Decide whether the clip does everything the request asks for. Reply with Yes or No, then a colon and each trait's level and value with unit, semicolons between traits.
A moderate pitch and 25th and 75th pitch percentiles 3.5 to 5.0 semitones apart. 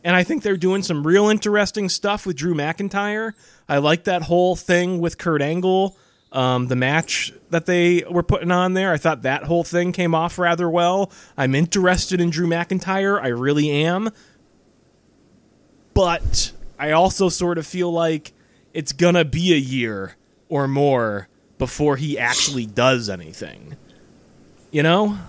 Yes: medium, 170 Hz; average, 4.2 semitones